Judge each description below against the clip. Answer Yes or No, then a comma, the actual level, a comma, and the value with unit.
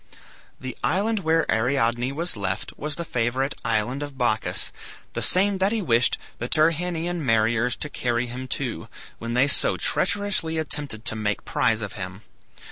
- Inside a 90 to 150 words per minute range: No, average, 160 wpm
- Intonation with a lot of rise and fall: Yes, wide, 5.9 semitones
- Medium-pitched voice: No, low, 130 Hz